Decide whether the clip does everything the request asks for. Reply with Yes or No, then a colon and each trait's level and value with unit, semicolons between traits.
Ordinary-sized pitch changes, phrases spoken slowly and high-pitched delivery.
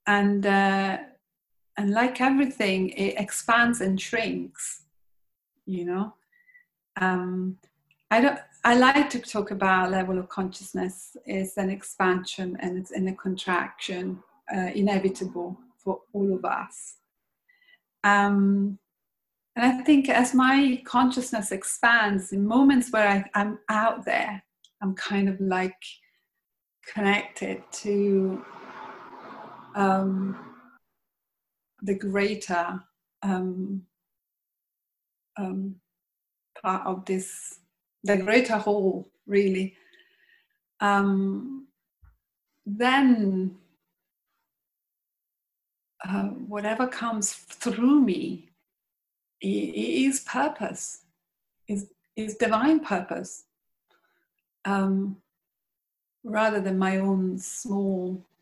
Yes: average, 3.6 semitones; slow, 90 wpm; high, 200 Hz